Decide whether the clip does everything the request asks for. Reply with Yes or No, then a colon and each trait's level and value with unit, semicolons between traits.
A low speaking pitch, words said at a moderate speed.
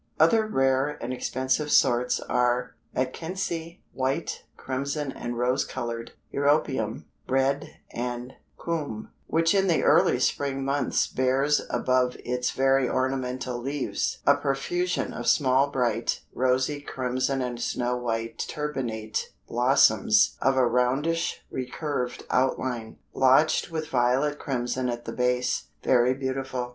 No: low, 130 Hz; slow, 120 wpm